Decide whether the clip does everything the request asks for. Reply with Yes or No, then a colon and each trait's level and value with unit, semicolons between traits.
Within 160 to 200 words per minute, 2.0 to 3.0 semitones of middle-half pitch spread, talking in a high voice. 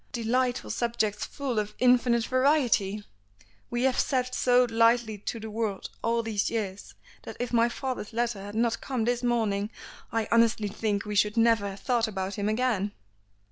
Yes: average, 170 wpm; narrow, 2.6 semitones; high, 230 Hz